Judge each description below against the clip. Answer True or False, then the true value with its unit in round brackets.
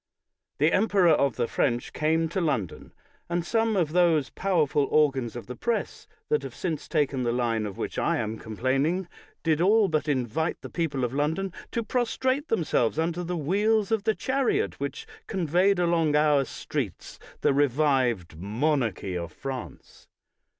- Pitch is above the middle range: False (155 Hz)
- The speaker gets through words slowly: False (160 wpm)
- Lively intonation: True (6.0 semitones)